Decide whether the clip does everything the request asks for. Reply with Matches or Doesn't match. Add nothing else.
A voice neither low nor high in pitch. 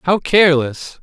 Matches